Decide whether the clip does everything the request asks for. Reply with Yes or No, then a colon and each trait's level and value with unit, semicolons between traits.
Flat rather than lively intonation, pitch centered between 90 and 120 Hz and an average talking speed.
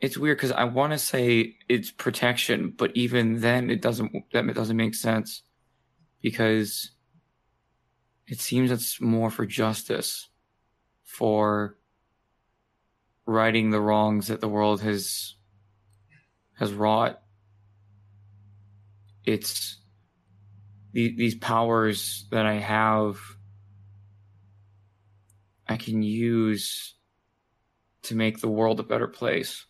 No: narrow, 2.0 semitones; low, 110 Hz; slow, 105 wpm